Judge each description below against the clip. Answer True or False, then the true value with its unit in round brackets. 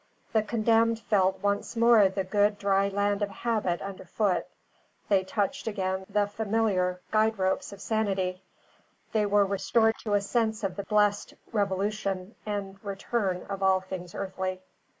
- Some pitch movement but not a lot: False (2.1 semitones)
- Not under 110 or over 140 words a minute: False (150 wpm)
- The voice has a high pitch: True (200 Hz)